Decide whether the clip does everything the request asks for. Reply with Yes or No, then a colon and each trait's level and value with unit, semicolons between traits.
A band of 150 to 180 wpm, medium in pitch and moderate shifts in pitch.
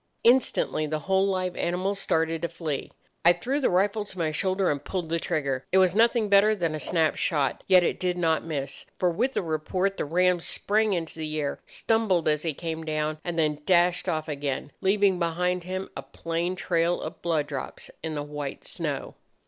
No: average, 200 wpm; medium, 170 Hz; average, 3.3 semitones